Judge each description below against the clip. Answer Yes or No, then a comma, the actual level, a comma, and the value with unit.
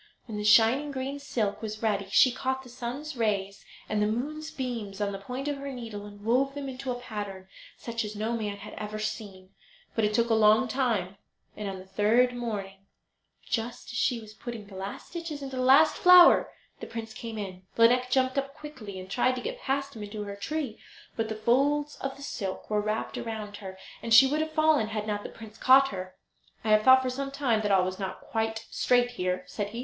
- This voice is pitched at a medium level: No, high, 225 Hz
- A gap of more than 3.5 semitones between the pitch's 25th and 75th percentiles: Yes, average, 4.1 semitones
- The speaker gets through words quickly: Yes, fast, 225 wpm